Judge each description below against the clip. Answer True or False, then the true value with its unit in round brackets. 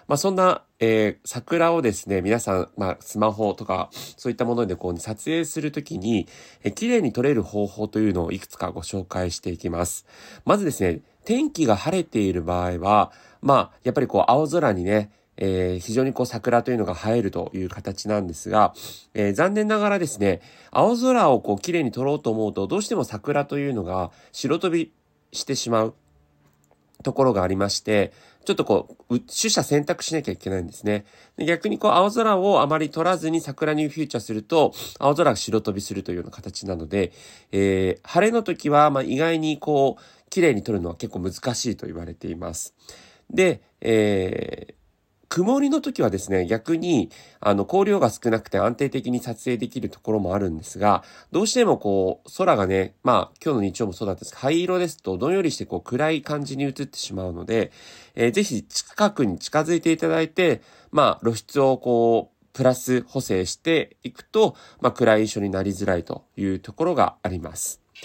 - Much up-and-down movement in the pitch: True (7.9 semitones)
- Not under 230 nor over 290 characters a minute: False (370 characters per minute)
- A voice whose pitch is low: True (115 Hz)